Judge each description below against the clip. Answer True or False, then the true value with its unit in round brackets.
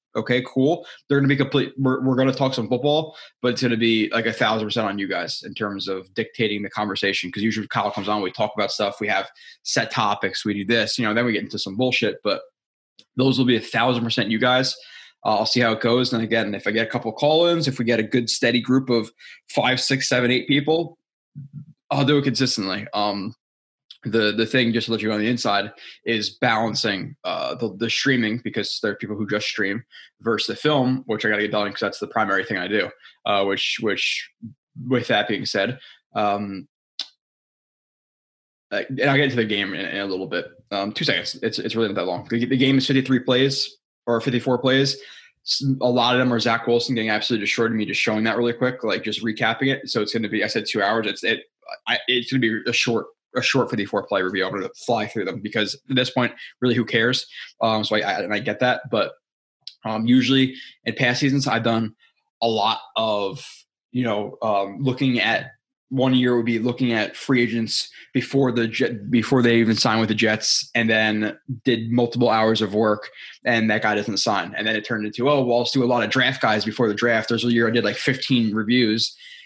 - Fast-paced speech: True (230 wpm)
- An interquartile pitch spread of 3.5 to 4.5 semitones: False (2.9 semitones)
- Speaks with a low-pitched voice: True (120 Hz)